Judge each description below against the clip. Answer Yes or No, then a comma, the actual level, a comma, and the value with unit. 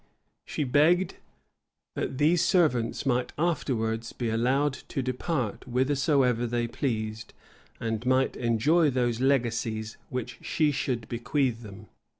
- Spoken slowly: Yes, slow, 120 wpm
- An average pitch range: Yes, average, 3.6 semitones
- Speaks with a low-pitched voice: Yes, low, 125 Hz